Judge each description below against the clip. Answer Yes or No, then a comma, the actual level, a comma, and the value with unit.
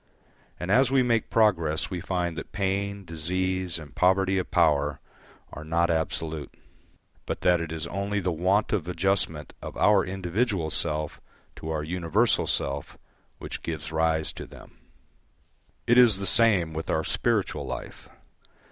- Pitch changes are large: No, average, 3.5 semitones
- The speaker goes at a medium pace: Yes, average, 145 wpm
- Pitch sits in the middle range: No, very low, 90 Hz